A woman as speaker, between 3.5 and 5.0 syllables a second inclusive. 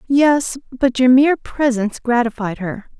Yes: female; 4.6 syllables/s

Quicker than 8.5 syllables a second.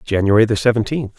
No: 6.5 syllables/s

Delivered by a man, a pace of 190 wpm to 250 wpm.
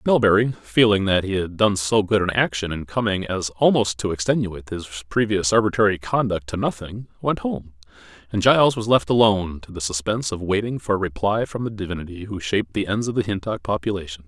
Yes: male; average, 200 wpm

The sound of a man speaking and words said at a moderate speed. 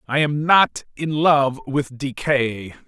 Yes: male; average, 145 wpm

